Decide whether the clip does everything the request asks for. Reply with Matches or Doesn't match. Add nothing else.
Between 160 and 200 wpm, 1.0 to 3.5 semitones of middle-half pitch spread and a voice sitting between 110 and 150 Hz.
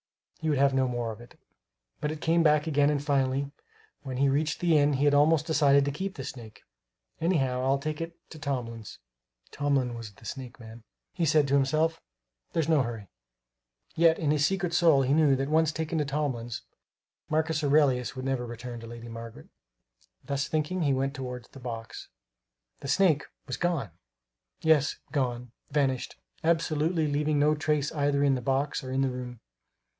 Matches